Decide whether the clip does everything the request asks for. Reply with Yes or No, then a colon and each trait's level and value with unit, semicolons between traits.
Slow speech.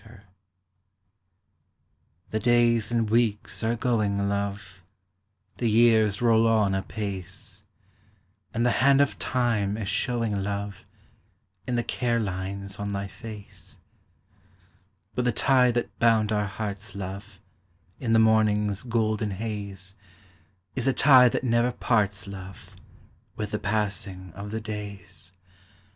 Yes: slow, 125 wpm